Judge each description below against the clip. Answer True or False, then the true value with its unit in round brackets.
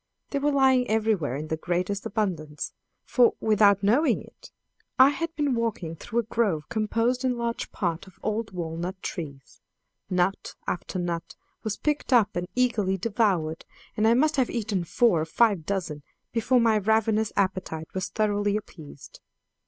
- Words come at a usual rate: True (160 wpm)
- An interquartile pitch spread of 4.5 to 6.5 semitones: True (4.9 semitones)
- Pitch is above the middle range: True (210 Hz)